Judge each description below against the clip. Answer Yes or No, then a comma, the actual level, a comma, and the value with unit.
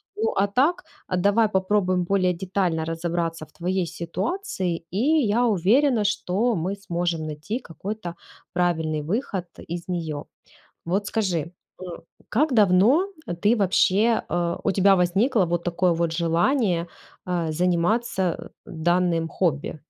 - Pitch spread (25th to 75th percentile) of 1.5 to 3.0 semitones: No, average, 3.7 semitones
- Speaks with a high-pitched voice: No, medium, 180 Hz